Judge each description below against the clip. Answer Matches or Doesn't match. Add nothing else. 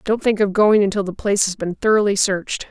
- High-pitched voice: Matches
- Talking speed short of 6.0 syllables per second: Doesn't match